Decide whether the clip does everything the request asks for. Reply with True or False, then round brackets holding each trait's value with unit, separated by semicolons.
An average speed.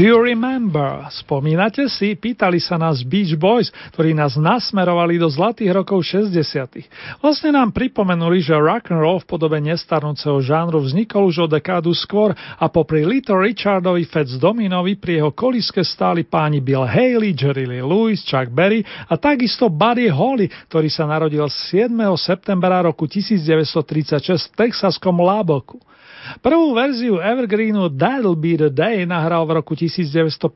True (145 wpm)